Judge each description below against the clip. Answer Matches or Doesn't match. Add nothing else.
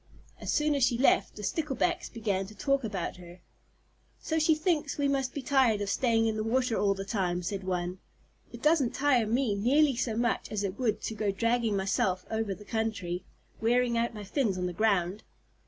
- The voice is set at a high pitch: Matches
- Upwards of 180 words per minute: Matches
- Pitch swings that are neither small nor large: Matches